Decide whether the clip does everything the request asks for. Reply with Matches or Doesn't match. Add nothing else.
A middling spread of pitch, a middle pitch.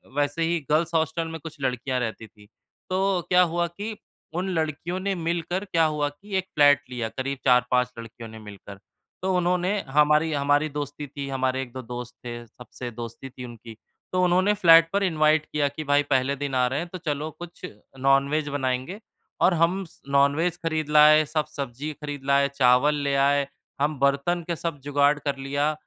Matches